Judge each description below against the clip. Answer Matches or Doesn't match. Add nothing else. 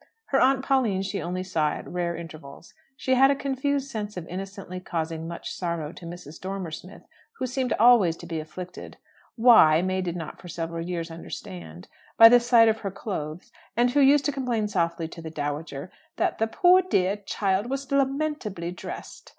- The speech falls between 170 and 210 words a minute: Matches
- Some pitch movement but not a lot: Doesn't match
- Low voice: Doesn't match